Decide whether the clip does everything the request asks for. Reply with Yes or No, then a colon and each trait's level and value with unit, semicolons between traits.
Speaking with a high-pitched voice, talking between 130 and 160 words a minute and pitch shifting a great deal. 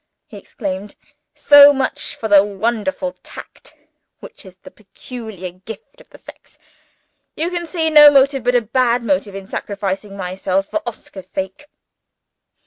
Yes: high, 220 Hz; average, 150 wpm; wide, 5.9 semitones